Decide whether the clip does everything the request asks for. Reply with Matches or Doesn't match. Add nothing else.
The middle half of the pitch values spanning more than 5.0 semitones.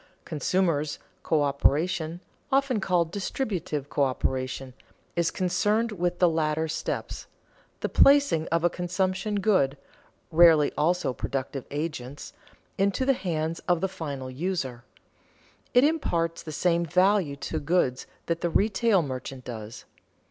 Doesn't match